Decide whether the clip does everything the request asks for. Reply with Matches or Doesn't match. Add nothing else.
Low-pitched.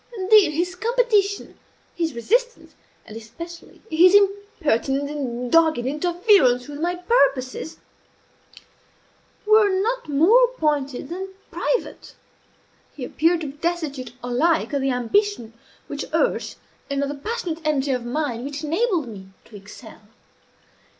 Doesn't match